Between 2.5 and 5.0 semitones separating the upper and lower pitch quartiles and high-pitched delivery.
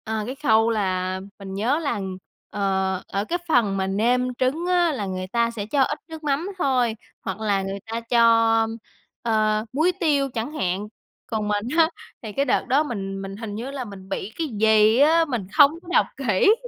No: wide, 5.5 semitones; high, 225 Hz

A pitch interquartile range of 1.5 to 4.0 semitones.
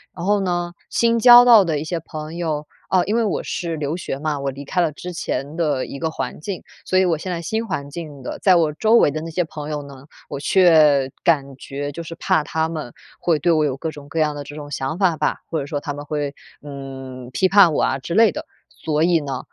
Yes: average, 3.4 semitones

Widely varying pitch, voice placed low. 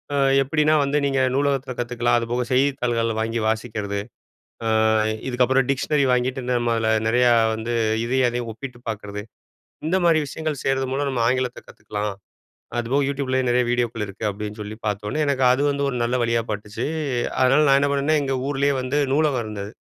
No: average, 3.3 semitones; low, 125 Hz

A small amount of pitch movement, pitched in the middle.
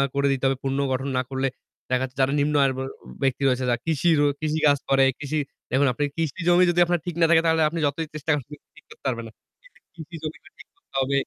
No: average, 3.3 semitones; medium, 145 Hz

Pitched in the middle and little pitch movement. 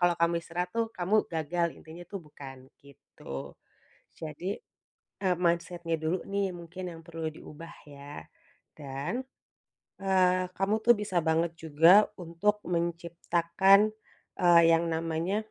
Yes: medium, 170 Hz; narrow, 2.2 semitones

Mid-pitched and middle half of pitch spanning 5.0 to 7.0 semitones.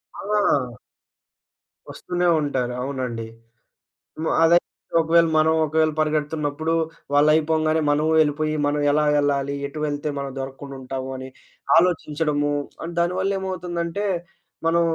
No: medium, 155 Hz; average, 2.7 semitones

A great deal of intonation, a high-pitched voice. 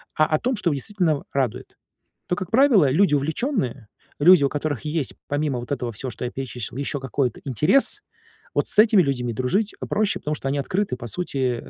No: wide, 6.0 semitones; medium, 145 Hz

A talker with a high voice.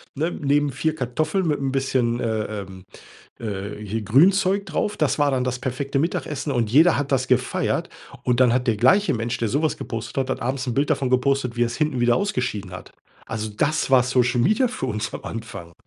No: low, 130 Hz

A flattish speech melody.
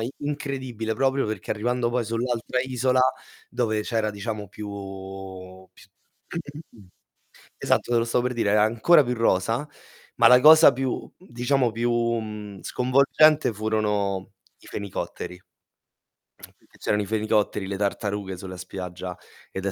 No: average, 3.2 semitones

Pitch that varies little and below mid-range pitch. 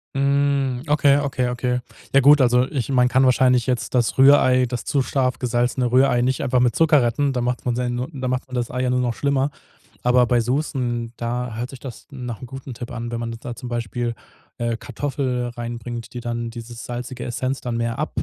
Yes: narrow, 1.7 semitones; low, 125 Hz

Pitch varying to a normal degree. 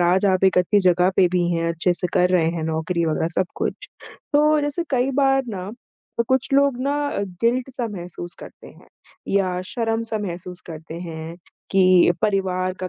Yes: average, 5.0 semitones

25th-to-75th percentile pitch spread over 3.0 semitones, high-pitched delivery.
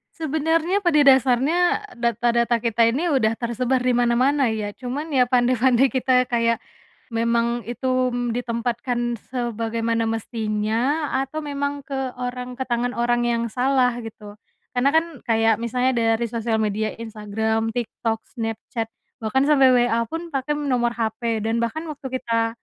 No: narrow, 2.6 semitones; high, 240 Hz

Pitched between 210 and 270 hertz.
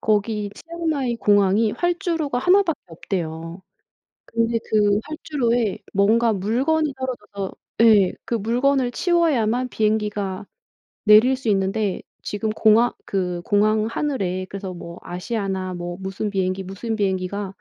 Yes: high, 215 Hz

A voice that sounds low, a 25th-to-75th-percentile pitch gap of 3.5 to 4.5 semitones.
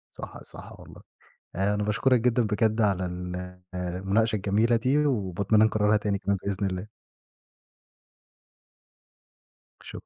No: low, 105 Hz; average, 3.0 semitones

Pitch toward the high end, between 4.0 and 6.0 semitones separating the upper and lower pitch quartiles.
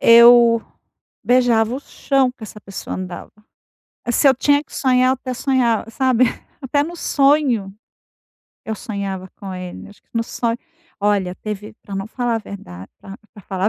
Yes: high, 230 Hz; average, 4.4 semitones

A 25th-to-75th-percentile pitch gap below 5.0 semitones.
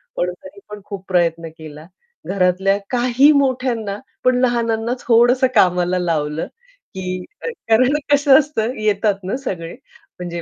No: wide, 5.6 semitones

